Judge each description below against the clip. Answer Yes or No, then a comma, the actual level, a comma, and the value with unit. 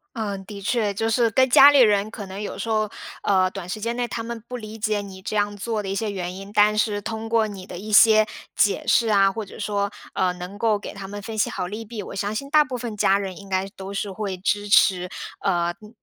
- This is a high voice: Yes, high, 205 Hz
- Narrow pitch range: Yes, narrow, 2.2 semitones